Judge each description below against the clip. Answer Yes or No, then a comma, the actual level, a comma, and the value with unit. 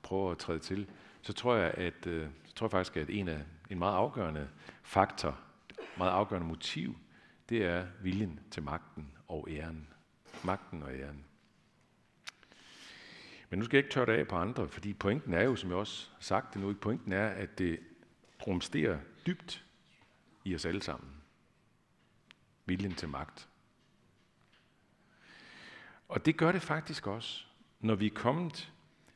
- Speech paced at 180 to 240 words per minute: No, average, 155 wpm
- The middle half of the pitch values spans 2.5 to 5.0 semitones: No, wide, 5.4 semitones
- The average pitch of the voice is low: Yes, very low, 95 Hz